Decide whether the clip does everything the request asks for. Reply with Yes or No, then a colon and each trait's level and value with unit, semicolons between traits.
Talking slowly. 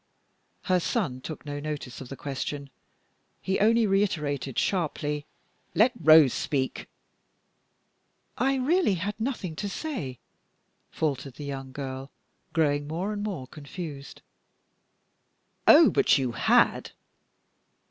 Yes: slow, 115 wpm